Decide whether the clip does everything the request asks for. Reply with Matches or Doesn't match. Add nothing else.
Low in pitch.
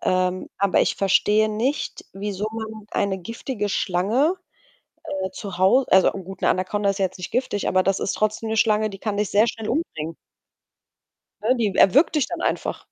Doesn't match